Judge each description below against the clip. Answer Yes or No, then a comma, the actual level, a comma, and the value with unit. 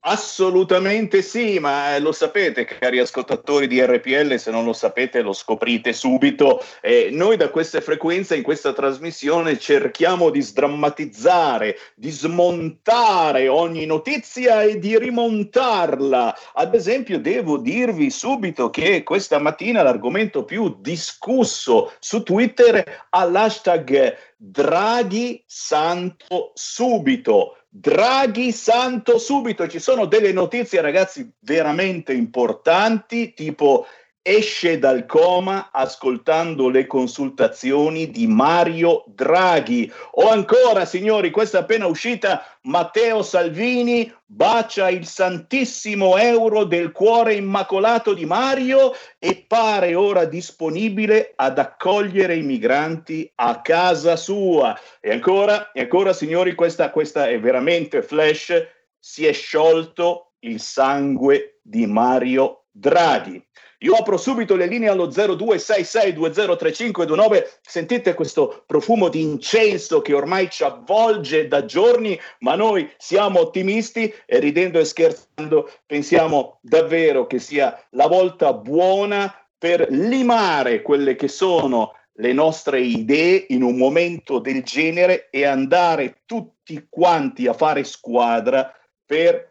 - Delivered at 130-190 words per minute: No, slow, 115 wpm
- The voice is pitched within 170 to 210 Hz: Yes, medium, 185 Hz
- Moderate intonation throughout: No, wide, 6.7 semitones